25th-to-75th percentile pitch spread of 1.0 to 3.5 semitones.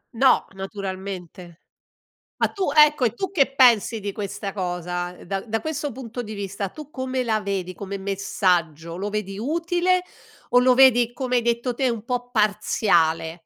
No: average, 5.0 semitones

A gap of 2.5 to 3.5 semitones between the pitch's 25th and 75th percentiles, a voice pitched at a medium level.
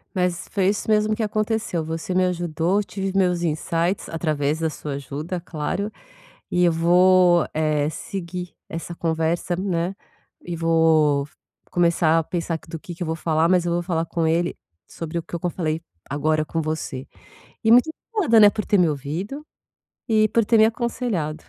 Yes: average, 2.9 semitones; medium, 170 Hz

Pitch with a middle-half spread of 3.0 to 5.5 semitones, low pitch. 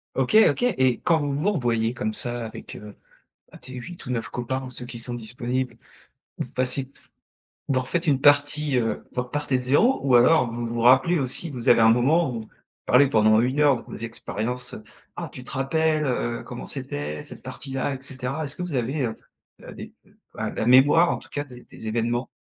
Yes: average, 3.3 semitones; low, 125 Hz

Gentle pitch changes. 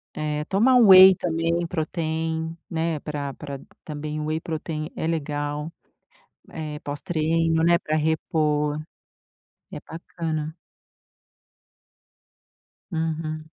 Yes: narrow, 1.5 semitones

